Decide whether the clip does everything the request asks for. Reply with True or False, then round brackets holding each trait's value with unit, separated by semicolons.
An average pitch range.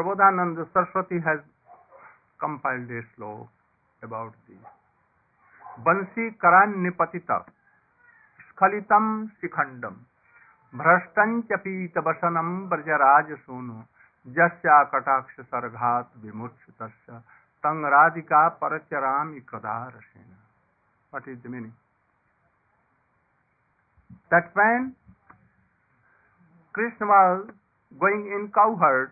False (7.3 semitones)